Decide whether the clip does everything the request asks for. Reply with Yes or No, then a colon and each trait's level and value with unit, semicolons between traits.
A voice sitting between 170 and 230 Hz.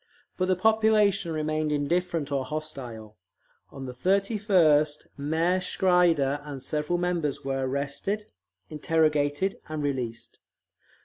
No: medium, 155 Hz